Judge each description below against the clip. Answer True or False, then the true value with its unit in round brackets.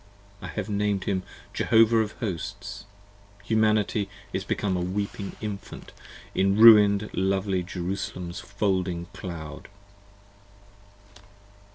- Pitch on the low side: True (100 Hz)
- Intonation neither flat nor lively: False (2.3 semitones)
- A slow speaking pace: True (95 wpm)